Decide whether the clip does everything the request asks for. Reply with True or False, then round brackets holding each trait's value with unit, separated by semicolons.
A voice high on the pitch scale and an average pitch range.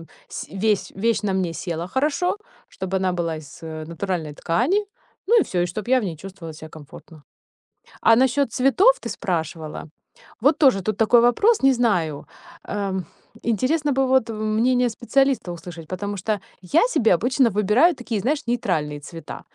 False (210 Hz; 6.8 semitones)